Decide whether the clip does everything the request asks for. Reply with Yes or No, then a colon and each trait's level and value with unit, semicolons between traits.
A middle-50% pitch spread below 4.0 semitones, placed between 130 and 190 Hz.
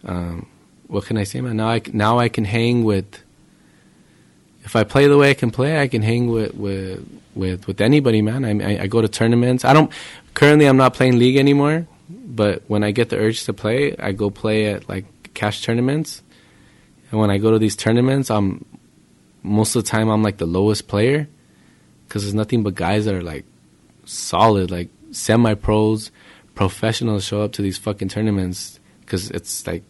No: average, 2.9 semitones; low, 110 Hz